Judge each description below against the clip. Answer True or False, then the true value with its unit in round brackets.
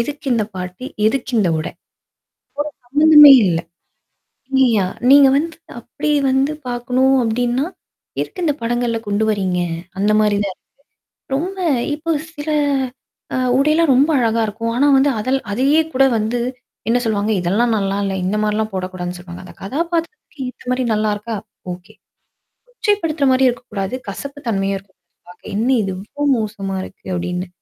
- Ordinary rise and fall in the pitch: False (5.7 semitones)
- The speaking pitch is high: True (230 Hz)